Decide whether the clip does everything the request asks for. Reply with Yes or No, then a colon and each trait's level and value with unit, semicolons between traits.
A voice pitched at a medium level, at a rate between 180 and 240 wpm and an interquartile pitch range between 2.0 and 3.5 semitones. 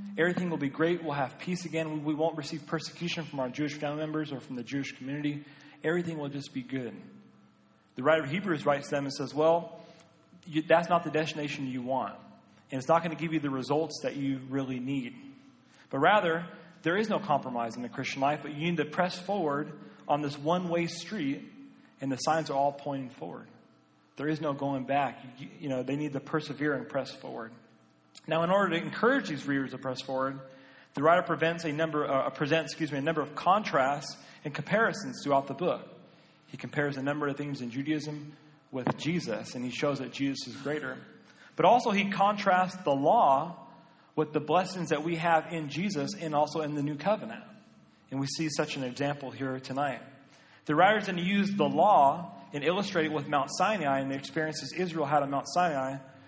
Yes: medium, 150 Hz; fast, 205 wpm; average, 3.2 semitones